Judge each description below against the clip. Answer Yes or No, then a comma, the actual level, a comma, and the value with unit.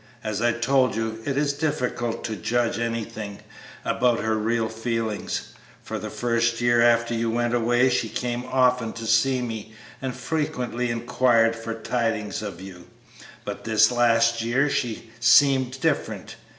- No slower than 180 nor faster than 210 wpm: No, average, 155 wpm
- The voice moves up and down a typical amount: No, narrow, 1.7 semitones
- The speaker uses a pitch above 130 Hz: No, low, 115 Hz